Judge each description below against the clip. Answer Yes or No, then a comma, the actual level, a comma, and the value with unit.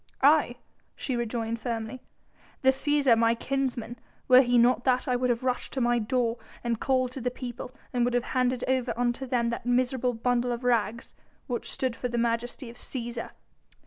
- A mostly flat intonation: Yes, narrow, 1.4 semitones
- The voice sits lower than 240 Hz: No, high, 245 Hz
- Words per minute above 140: Yes, average, 185 wpm